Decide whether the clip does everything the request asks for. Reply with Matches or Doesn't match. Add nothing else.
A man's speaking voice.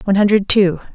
Doesn't match